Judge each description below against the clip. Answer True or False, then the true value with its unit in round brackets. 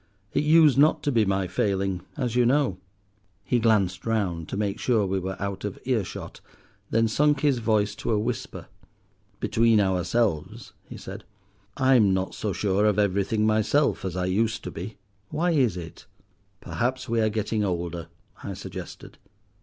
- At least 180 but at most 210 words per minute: False (165 wpm)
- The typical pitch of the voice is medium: False (105 Hz)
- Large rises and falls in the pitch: False (4.1 semitones)